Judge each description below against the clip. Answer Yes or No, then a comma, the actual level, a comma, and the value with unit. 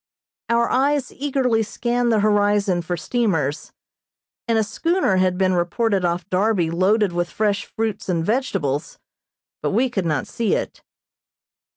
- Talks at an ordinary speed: Yes, average, 145 wpm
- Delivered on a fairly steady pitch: No, average, 4.7 semitones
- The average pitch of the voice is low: No, high, 205 Hz